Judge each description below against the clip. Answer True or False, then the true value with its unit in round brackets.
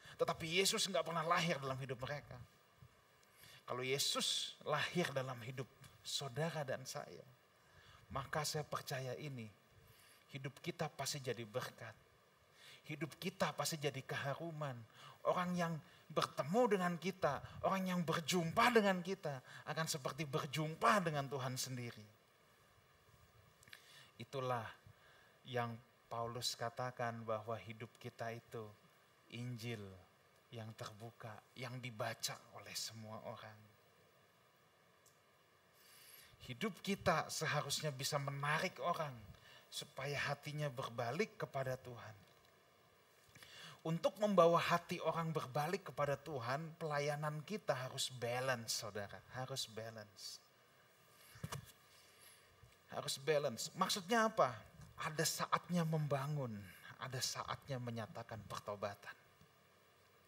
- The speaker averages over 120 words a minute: False (100 wpm)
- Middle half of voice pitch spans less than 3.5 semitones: False (5.2 semitones)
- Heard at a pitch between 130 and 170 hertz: True (140 Hz)